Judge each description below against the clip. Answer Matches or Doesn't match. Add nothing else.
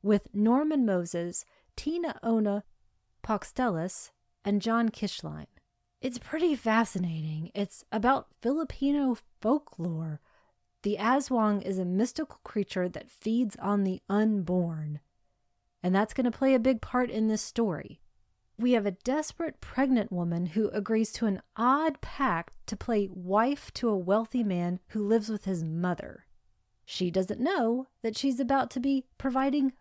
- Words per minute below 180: Matches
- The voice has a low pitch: Doesn't match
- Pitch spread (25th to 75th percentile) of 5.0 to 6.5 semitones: Matches